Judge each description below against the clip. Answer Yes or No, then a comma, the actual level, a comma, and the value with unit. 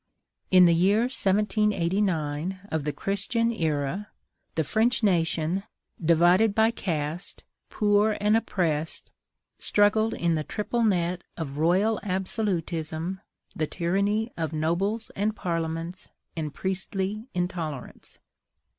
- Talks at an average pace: No, slow, 110 wpm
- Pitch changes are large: No, average, 4.3 semitones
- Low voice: No, medium, 185 Hz